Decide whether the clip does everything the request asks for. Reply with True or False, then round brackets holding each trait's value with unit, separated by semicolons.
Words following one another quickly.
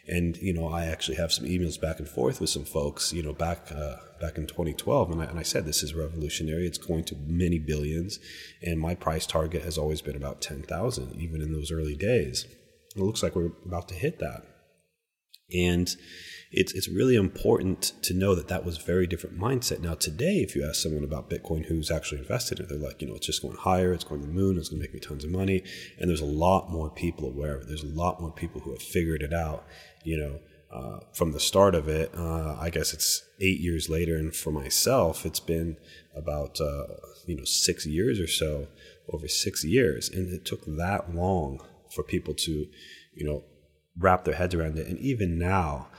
True (225 wpm)